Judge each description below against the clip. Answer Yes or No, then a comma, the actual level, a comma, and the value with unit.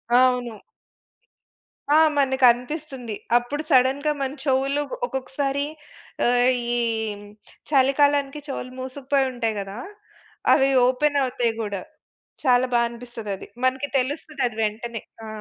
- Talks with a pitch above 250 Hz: Yes, very high, 260 Hz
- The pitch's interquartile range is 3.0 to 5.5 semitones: No, narrow, 2.4 semitones